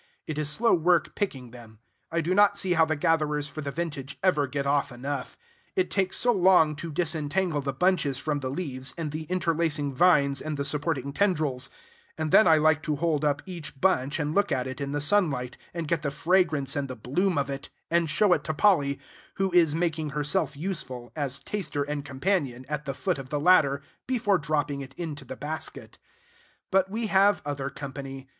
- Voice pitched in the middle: Yes, medium, 150 Hz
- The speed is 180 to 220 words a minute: Yes, average, 200 wpm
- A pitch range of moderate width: Yes, average, 4.0 semitones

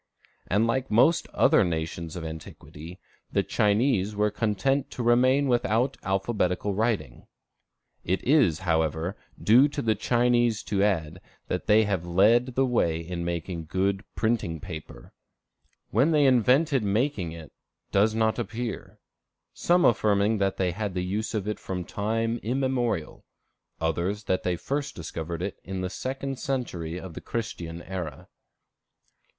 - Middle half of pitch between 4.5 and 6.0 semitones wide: Yes, average, 5.3 semitones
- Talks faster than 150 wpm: No, average, 140 wpm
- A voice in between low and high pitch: No, low, 105 Hz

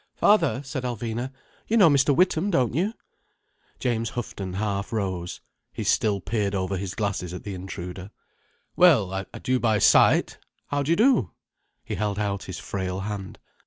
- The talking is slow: No, average, 160 wpm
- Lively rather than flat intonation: Yes, wide, 5.9 semitones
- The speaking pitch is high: No, low, 105 Hz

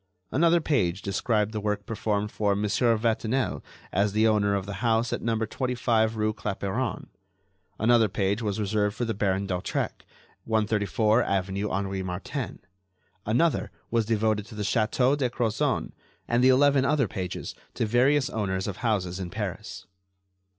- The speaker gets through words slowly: No, average, 150 wpm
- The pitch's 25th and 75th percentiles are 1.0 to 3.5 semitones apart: Yes, average, 2.9 semitones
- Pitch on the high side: No, low, 110 Hz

